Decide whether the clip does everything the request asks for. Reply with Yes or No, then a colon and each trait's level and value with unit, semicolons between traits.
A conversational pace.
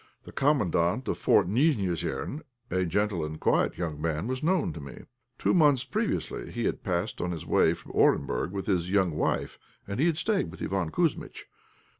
Yes: average, 185 wpm